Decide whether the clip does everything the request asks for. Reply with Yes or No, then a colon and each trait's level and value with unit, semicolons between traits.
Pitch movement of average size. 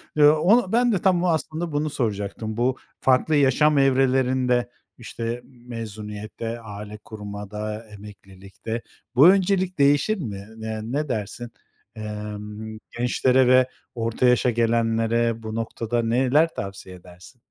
Yes: average, 4.2 semitones